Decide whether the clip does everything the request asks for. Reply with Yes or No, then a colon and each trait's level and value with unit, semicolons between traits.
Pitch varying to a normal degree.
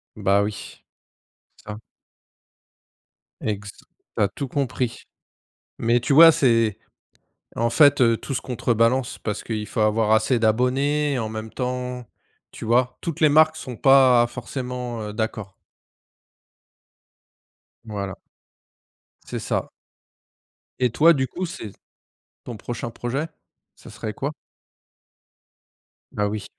Yes: average, 3.3 semitones